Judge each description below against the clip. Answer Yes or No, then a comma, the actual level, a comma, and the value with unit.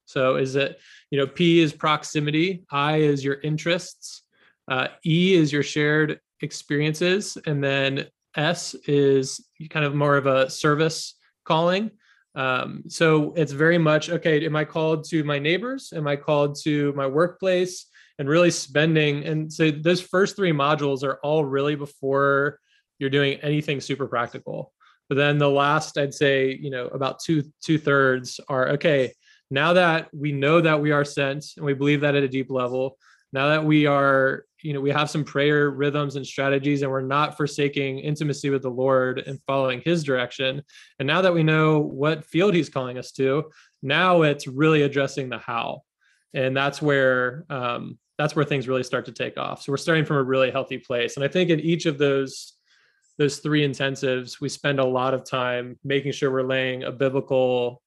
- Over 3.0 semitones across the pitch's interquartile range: No, narrow, 2.5 semitones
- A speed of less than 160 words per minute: No, average, 185 wpm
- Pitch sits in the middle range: Yes, medium, 145 Hz